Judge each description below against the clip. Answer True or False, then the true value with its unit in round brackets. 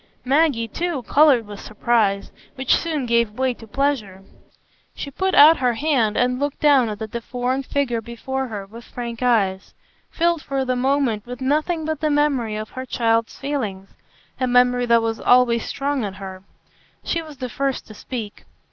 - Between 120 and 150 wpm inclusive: False (175 wpm)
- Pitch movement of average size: True (3.8 semitones)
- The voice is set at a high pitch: True (250 Hz)